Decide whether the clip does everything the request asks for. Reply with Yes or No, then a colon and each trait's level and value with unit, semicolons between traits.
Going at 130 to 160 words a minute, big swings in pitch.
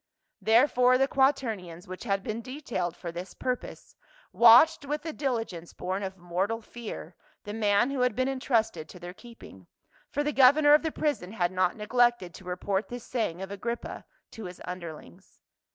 No: average, 175 wpm; wide, 5.7 semitones